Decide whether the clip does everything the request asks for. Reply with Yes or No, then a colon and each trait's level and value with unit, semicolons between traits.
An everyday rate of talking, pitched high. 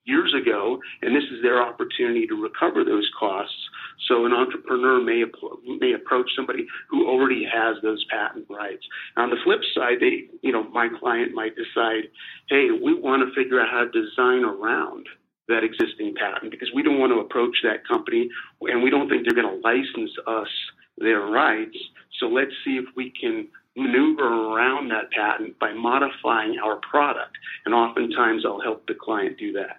Yes: average, 180 wpm; very high, 350 Hz